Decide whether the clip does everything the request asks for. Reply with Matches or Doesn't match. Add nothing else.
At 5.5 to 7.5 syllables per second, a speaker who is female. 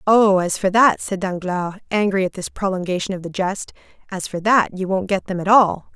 Doesn't match